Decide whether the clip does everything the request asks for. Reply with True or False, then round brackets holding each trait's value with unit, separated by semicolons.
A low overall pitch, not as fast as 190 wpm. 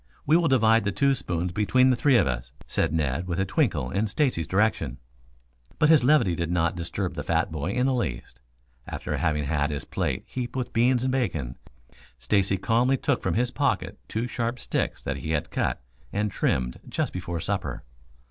False (100 Hz; 195 wpm)